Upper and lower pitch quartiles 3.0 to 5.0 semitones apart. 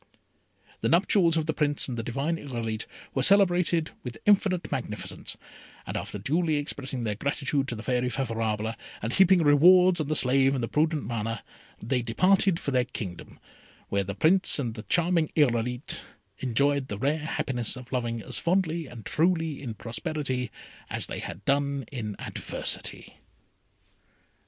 No: wide, 5.5 semitones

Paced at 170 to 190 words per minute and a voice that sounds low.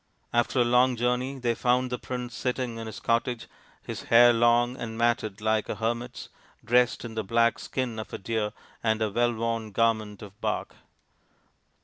Yes: average, 175 wpm; low, 115 Hz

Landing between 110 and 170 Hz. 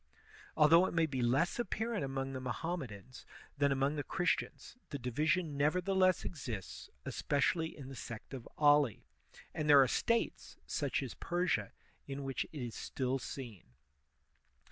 Yes: medium, 140 Hz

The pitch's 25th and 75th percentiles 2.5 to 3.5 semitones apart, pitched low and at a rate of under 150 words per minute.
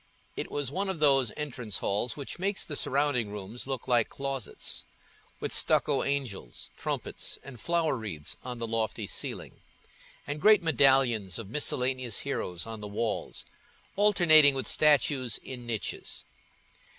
No: average, 4.4 semitones; low, 130 Hz; average, 140 wpm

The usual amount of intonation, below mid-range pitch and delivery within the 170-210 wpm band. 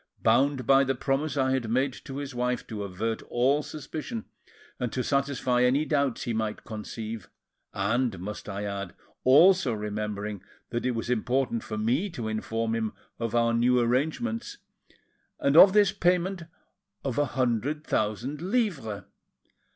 No: average, 4.4 semitones; low, 125 Hz; average, 150 wpm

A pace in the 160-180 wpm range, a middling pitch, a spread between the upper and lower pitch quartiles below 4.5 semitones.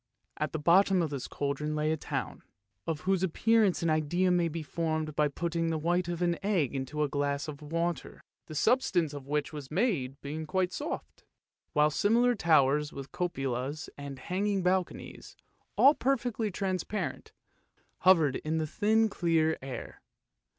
Yes: average, 165 wpm; medium, 160 Hz; average, 3.9 semitones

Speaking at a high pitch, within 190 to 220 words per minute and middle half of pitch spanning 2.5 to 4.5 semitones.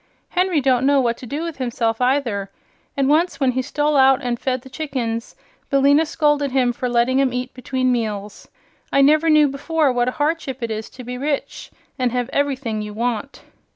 Yes: very high, 260 Hz; average, 195 wpm; average, 2.9 semitones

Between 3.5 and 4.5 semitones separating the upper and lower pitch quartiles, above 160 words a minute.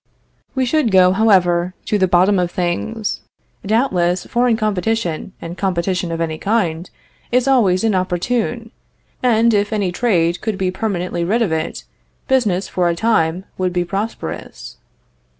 No: average, 4.1 semitones; average, 145 wpm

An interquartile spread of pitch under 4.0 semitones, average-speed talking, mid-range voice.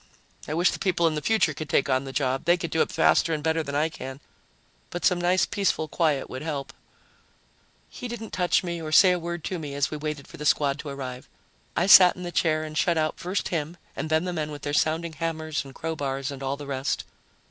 No: average, 3.3 semitones; fast, 245 wpm; medium, 155 Hz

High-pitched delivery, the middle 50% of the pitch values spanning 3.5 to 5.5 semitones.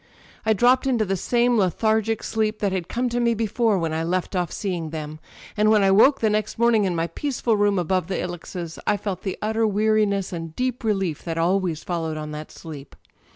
Yes: high, 195 Hz; average, 4.4 semitones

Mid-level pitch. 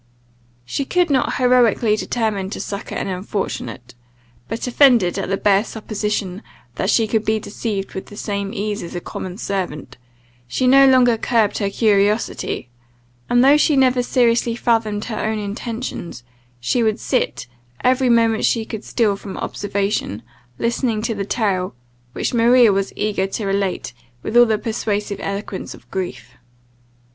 No: high, 215 Hz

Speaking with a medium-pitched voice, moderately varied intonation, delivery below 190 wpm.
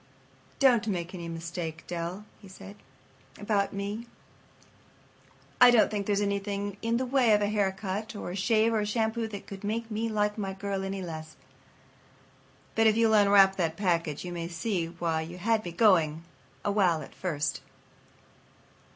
No: high, 200 Hz; average, 3.7 semitones; average, 170 wpm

